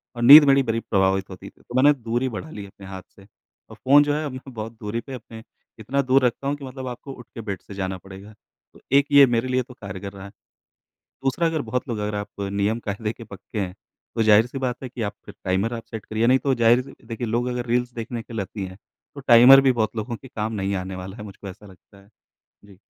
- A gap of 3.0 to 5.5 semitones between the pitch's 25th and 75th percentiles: Yes, average, 4.1 semitones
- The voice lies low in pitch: Yes, low, 115 Hz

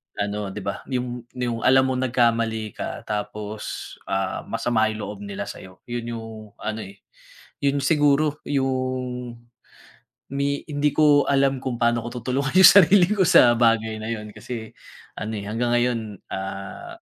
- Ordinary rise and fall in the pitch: Yes, average, 3.7 semitones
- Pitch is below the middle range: Yes, low, 120 Hz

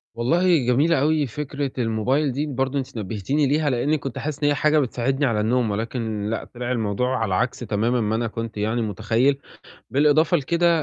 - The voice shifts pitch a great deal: No, average, 4.4 semitones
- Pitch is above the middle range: No, low, 125 Hz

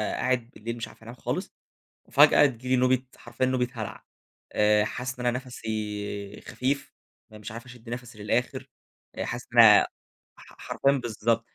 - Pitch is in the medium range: No, low, 120 Hz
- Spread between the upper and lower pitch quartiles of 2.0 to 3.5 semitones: Yes, average, 2.8 semitones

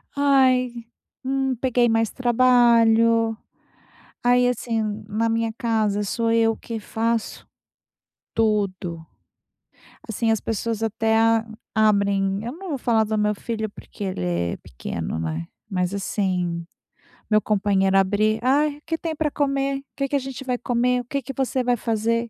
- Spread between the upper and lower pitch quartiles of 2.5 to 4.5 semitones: Yes, average, 3.1 semitones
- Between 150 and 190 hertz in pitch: No, high, 225 Hz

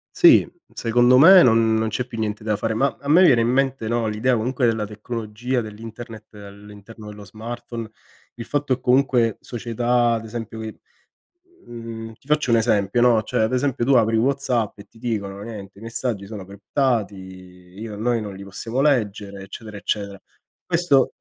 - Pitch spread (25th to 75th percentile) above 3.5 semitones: No, average, 2.7 semitones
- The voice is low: Yes, low, 115 Hz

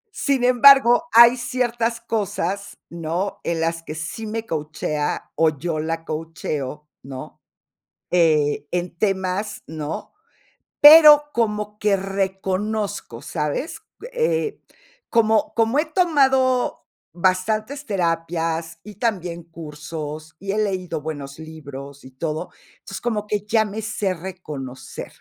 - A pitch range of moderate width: No, wide, 5.8 semitones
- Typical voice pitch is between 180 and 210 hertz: Yes, high, 190 Hz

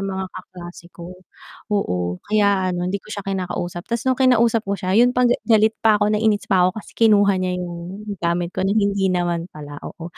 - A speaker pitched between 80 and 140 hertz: No, high, 195 Hz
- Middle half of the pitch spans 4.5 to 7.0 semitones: No, average, 3.2 semitones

